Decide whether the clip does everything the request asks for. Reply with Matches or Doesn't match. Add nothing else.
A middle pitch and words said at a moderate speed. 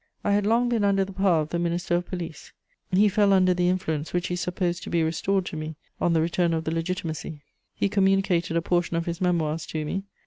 Doesn't match